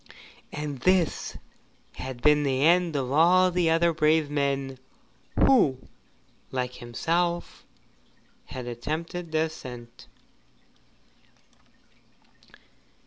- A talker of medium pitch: Yes, medium, 150 Hz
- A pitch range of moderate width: Yes, average, 4.4 semitones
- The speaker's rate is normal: No, slow, 85 wpm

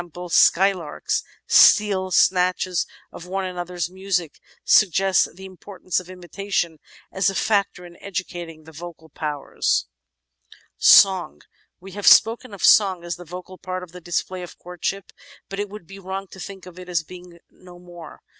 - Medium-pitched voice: Yes, medium, 180 Hz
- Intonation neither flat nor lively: No, narrow, 1.8 semitones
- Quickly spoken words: No, average, 155 wpm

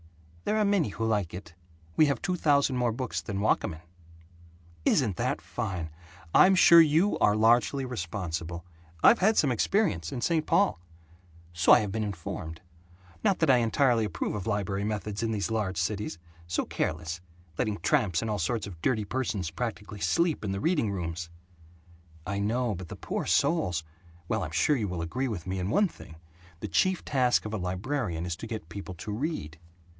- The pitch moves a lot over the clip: Yes, wide, 6.6 semitones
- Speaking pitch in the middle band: No, low, 105 Hz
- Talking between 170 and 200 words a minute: Yes, average, 185 wpm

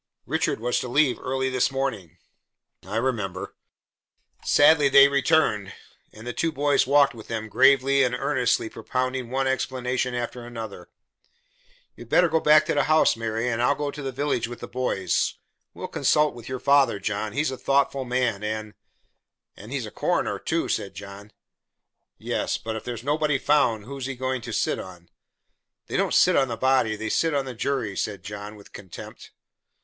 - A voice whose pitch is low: Yes, low, 125 Hz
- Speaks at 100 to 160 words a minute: No, average, 185 wpm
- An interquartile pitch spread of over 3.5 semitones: Yes, average, 3.9 semitones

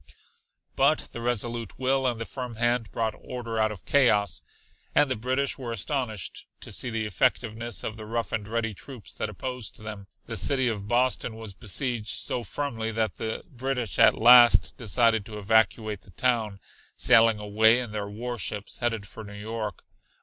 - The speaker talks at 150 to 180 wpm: Yes, average, 170 wpm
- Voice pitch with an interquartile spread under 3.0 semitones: Yes, narrow, 2.4 semitones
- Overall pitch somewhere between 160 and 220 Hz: No, low, 115 Hz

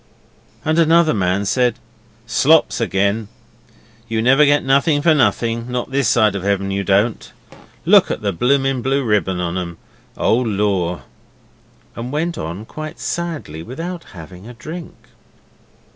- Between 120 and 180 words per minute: Yes, average, 145 wpm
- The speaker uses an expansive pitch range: Yes, wide, 6.2 semitones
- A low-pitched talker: Yes, low, 115 Hz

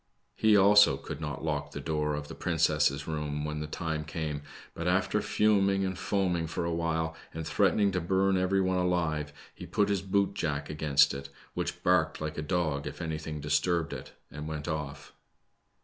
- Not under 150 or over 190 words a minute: Yes, average, 180 wpm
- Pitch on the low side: Yes, very low, 80 Hz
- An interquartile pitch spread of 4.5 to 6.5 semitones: No, average, 3.6 semitones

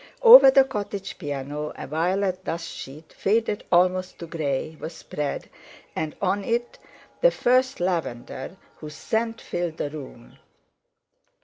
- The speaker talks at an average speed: No, slow, 130 wpm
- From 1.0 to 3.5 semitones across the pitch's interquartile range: No, wide, 5.5 semitones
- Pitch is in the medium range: Yes, medium, 175 Hz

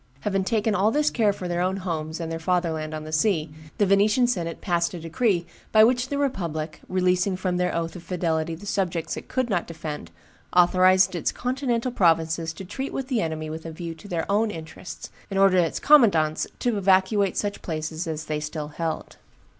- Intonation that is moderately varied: Yes, average, 4.0 semitones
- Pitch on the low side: No, medium, 180 Hz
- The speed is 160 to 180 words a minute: No, average, 200 wpm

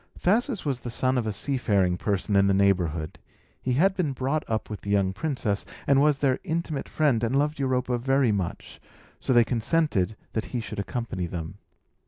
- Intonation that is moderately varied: No, wide, 5.8 semitones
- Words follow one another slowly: No, average, 190 wpm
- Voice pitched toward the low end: Yes, low, 120 Hz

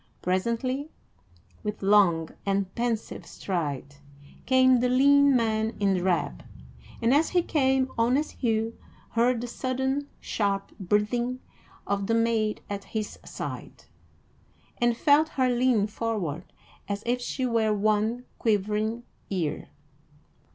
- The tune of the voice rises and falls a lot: No, average, 3.9 semitones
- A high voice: Yes, high, 230 Hz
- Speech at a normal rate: No, slow, 120 wpm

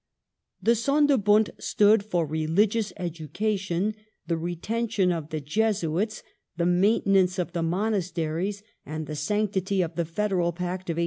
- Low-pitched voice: No, medium, 185 Hz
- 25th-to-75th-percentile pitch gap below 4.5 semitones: Yes, average, 3.9 semitones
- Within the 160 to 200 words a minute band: No, slow, 135 wpm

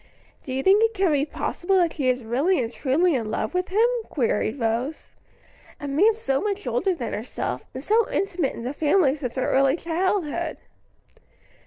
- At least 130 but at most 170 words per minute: No, average, 185 wpm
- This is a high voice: Yes, very high, 300 Hz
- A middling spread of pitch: No, wide, 6.6 semitones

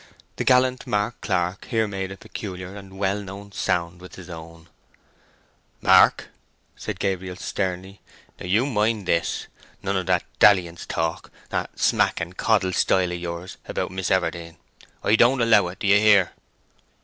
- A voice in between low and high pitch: No, very low, 95 Hz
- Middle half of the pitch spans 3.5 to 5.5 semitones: No, narrow, 2.6 semitones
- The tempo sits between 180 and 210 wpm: No, average, 150 wpm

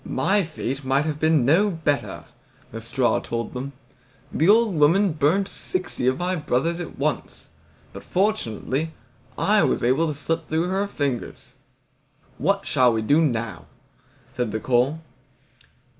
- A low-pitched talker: No, medium, 150 Hz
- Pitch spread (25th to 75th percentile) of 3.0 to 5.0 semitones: No, wide, 5.5 semitones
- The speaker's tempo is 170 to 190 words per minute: No, average, 145 wpm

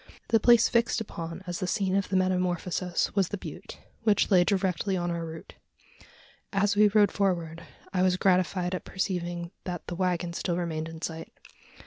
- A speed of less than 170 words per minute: No, average, 175 wpm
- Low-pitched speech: No, medium, 180 Hz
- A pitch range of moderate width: No, narrow, 2.2 semitones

